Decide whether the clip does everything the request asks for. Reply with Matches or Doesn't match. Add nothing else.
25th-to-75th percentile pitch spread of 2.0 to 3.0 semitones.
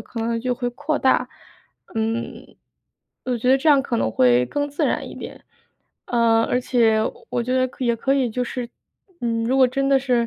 Matches